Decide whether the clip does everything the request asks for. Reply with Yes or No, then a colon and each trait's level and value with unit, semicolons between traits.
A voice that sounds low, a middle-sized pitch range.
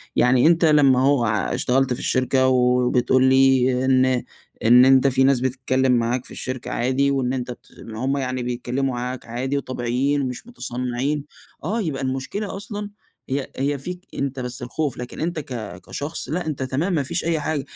No: low, 130 Hz; narrow, 2.2 semitones